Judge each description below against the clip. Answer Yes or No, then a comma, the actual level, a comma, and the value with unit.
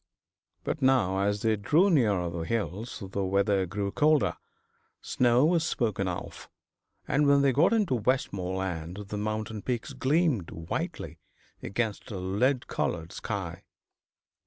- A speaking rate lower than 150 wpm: Yes, slow, 135 wpm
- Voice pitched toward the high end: No, low, 110 Hz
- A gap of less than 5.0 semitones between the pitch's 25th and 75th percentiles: No, wide, 5.6 semitones